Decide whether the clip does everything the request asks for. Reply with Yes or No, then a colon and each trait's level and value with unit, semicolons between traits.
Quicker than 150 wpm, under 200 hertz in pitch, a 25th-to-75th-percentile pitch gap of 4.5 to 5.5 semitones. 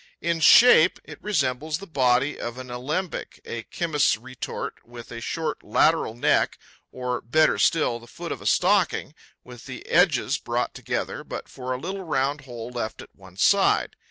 Yes: average, 170 wpm; low, 135 Hz; average, 5.1 semitones